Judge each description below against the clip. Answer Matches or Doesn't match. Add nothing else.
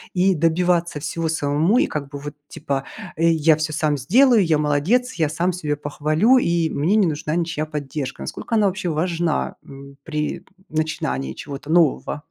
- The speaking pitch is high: Doesn't match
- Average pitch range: Matches